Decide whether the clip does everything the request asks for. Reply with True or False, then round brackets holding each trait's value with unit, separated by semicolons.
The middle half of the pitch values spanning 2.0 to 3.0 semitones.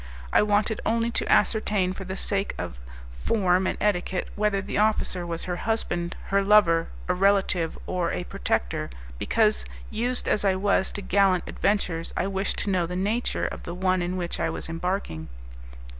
True (2.7 semitones)